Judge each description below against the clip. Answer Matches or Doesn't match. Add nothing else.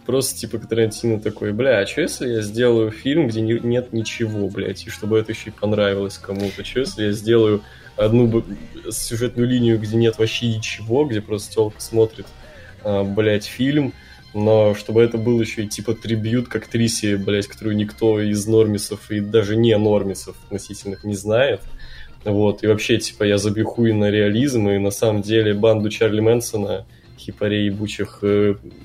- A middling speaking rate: Doesn't match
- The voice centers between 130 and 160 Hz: Doesn't match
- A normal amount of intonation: Doesn't match